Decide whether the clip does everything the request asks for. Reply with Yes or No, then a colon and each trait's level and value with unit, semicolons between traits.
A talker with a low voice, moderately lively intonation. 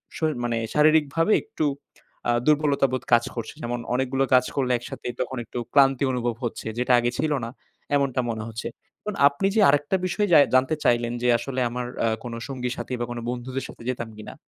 Yes: low, 130 Hz; average, 3.0 semitones